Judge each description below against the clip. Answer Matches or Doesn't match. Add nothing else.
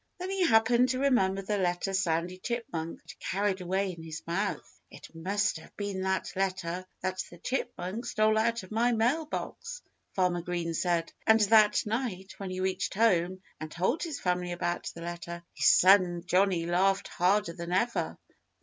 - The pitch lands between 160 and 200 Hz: Matches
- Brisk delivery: Doesn't match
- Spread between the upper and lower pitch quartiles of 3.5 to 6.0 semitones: Matches